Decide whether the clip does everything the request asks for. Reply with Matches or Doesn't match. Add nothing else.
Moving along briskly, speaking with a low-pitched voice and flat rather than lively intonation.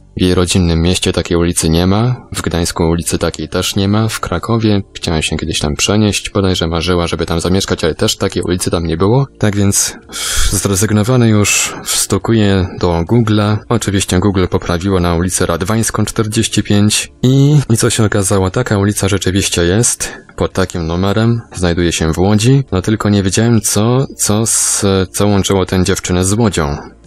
Doesn't match